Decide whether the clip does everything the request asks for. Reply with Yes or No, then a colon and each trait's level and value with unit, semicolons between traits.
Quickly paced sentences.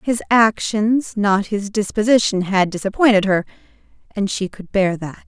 No: average, 150 wpm